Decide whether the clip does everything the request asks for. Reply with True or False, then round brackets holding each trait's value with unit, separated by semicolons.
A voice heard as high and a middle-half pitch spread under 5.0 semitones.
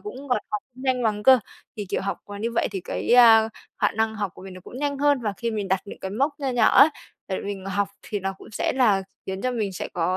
True (220 Hz; 4.5 semitones)